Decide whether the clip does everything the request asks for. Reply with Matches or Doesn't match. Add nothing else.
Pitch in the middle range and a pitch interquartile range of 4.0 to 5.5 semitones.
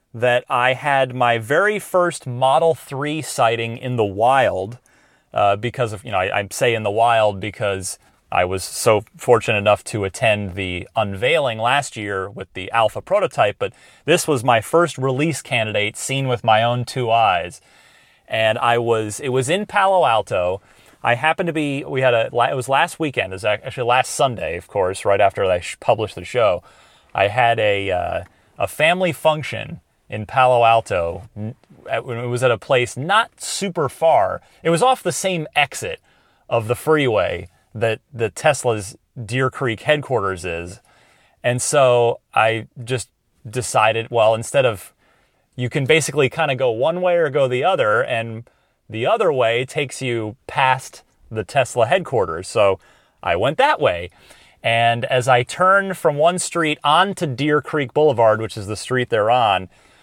Doesn't match